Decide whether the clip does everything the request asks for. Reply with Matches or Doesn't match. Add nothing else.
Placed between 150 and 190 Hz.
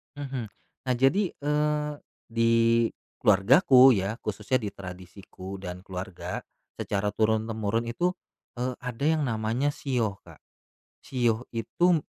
Doesn't match